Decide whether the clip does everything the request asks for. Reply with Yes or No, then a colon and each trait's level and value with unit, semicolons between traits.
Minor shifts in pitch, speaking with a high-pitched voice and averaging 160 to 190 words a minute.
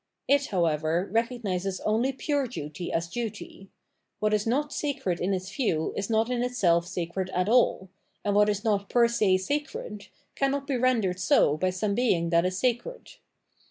No: average, 5.2 semitones; high, 205 Hz; average, 170 wpm